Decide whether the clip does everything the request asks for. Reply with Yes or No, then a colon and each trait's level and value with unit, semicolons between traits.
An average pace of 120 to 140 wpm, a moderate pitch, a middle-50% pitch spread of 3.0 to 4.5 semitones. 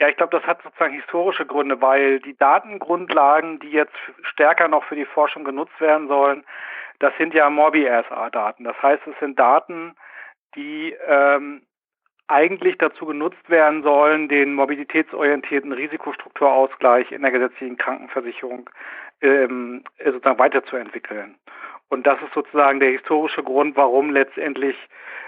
No: average, 135 wpm; medium, 145 Hz; narrow, 2.4 semitones